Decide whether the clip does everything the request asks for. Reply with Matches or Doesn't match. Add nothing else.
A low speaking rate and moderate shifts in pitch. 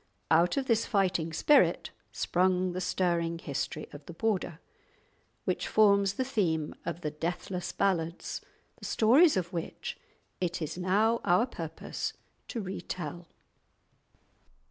Matches